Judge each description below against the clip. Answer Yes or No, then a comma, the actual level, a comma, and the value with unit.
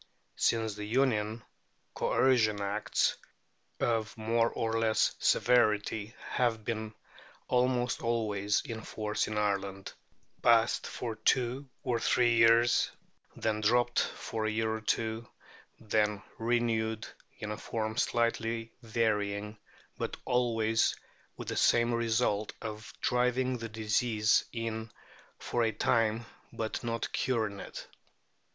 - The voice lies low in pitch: Yes, low, 115 Hz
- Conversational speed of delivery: No, slow, 120 wpm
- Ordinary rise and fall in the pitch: No, narrow, 1.6 semitones